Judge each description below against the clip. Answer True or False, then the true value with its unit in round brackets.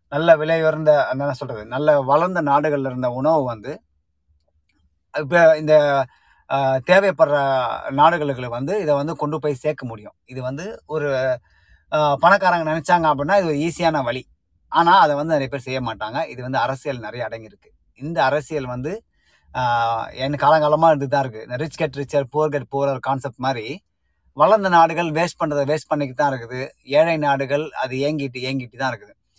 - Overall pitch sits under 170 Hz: True (140 Hz)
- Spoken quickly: True (150 wpm)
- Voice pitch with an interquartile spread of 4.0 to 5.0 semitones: False (3.2 semitones)